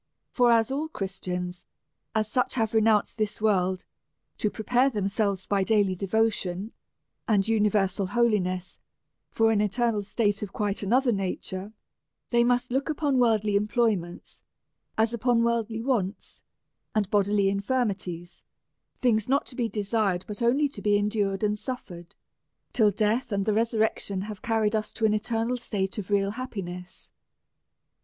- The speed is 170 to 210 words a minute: No, average, 150 wpm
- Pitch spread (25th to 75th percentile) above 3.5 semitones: No, average, 2.9 semitones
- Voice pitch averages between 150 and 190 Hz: No, high, 215 Hz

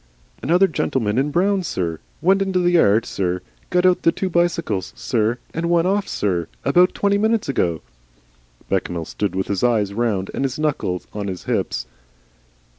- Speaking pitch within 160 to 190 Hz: No, low, 135 Hz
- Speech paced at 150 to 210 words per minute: Yes, average, 170 wpm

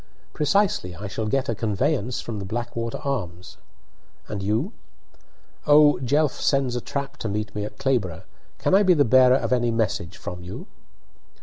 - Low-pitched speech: Yes, low, 120 Hz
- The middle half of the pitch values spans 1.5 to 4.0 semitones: No, average, 5.0 semitones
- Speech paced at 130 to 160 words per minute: No, average, 170 wpm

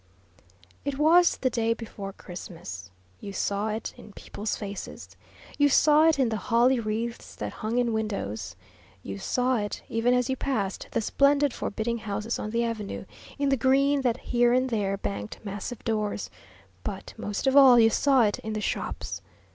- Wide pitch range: No, average, 3.9 semitones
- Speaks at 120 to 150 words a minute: No, average, 175 wpm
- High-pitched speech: Yes, high, 230 Hz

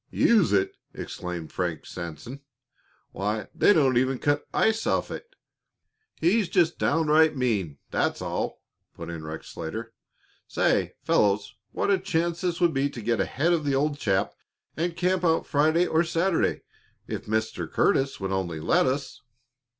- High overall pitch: No, medium, 140 Hz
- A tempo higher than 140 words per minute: Yes, average, 155 wpm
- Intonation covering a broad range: Yes, wide, 8.7 semitones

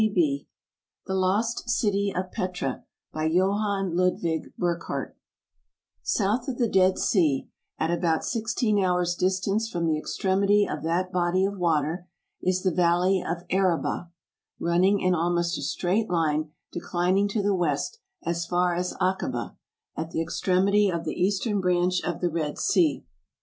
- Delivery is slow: No, average, 150 wpm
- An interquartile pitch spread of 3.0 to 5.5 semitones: No, narrow, 2.5 semitones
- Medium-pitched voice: Yes, medium, 180 Hz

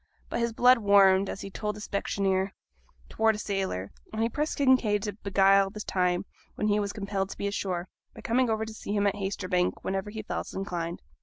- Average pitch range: No, narrow, 2.0 semitones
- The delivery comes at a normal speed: No, fast, 210 wpm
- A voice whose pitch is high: Yes, high, 200 Hz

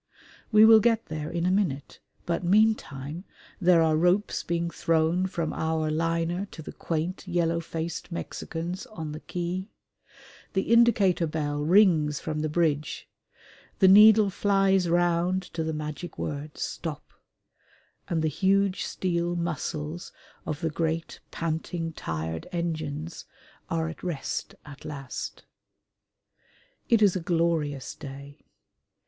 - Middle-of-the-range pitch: Yes, medium, 165 Hz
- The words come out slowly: Yes, slow, 130 wpm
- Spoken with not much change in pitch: No, average, 3.0 semitones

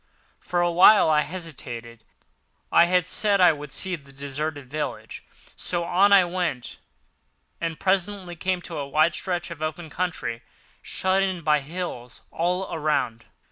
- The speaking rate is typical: Yes, average, 150 wpm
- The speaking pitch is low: No, medium, 170 Hz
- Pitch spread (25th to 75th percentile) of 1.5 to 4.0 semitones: Yes, average, 3.6 semitones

